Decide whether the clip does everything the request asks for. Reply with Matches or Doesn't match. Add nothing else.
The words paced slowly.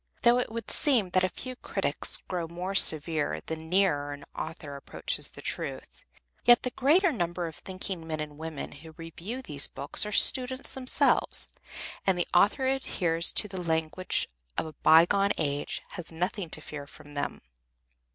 Doesn't match